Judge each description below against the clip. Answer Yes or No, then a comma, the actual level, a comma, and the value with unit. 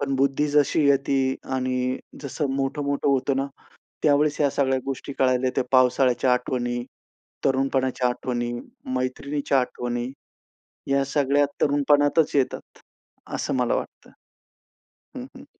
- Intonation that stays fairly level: Yes, narrow, 1.8 semitones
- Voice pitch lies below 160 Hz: Yes, low, 135 Hz